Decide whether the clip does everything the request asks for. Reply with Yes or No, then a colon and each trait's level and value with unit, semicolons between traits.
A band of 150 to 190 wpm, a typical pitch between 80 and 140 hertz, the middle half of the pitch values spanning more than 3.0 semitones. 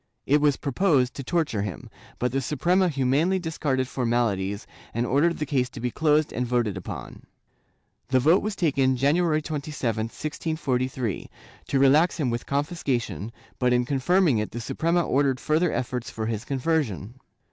Yes: average, 160 wpm; low, 135 Hz; average, 4.2 semitones